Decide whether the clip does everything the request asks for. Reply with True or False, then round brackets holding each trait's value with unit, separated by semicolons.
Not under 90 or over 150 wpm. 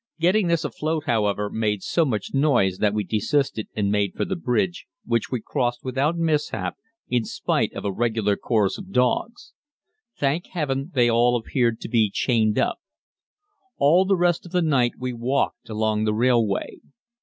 False (170 wpm)